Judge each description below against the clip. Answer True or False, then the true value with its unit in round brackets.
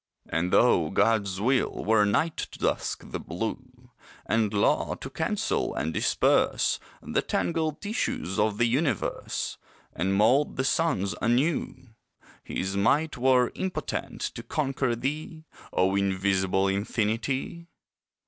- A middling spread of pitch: False (5.7 semitones)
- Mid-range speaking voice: False (115 Hz)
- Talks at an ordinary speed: False (120 wpm)